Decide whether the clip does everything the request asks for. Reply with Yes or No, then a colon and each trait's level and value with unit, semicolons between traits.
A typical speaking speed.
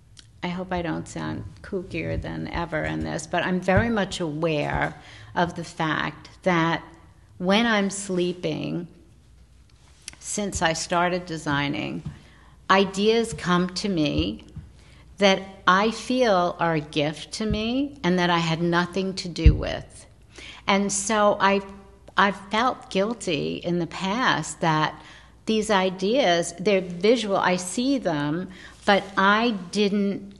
No: slow, 130 wpm